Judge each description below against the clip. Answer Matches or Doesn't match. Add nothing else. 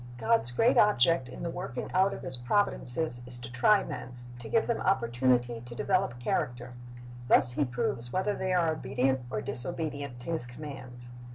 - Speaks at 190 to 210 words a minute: Doesn't match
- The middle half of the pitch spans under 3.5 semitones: Doesn't match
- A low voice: Matches